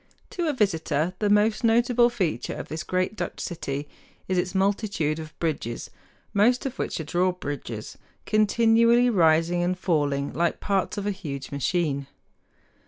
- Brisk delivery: No, average, 150 wpm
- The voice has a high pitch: No, medium, 180 Hz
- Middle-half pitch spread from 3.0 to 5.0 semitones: No, wide, 5.4 semitones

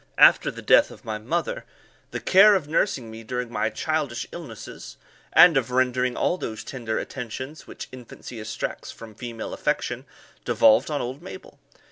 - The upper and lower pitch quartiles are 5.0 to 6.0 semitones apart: Yes, wide, 5.5 semitones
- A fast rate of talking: No, average, 160 wpm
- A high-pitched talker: No, low, 125 Hz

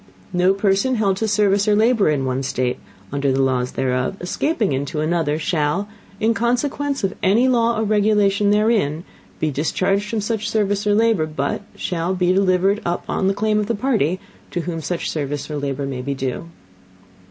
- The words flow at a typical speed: Yes, average, 180 wpm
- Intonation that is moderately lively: No, wide, 6.2 semitones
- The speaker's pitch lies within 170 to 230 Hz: Yes, high, 190 Hz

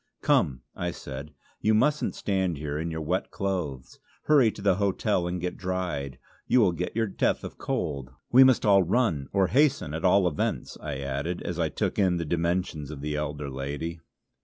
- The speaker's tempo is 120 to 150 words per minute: No, average, 190 wpm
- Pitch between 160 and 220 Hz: No, very low, 85 Hz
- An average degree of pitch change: Yes, average, 4.9 semitones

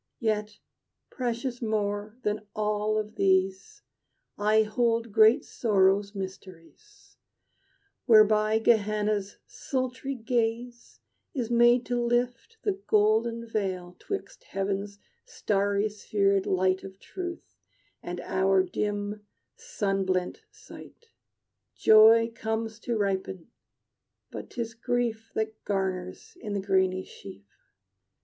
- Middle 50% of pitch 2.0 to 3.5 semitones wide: Yes, average, 3.0 semitones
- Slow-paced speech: Yes, slow, 105 wpm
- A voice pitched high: Yes, high, 215 Hz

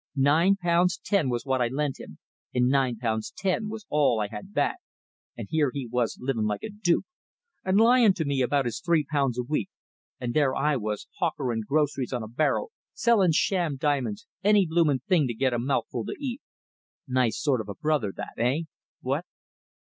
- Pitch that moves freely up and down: Yes, wide, 5.7 semitones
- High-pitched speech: No, medium, 140 Hz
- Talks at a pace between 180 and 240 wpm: Yes, average, 190 wpm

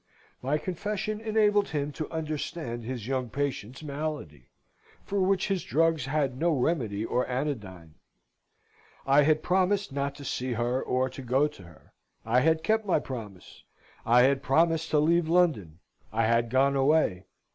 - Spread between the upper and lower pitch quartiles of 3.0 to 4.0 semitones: No, average, 4.8 semitones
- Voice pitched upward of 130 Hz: Yes, medium, 140 Hz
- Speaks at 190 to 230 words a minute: No, average, 155 wpm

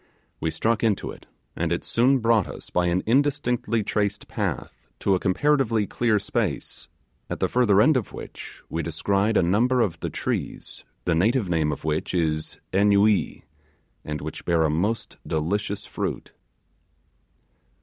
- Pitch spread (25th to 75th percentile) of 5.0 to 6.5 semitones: Yes, average, 5.3 semitones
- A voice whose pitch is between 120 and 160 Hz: No, low, 100 Hz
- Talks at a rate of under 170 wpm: Yes, average, 155 wpm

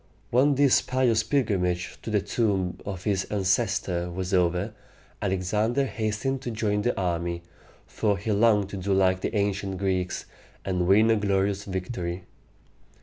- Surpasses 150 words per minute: No, average, 145 wpm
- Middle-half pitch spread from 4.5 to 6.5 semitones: No, average, 3.0 semitones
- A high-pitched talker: No, low, 100 Hz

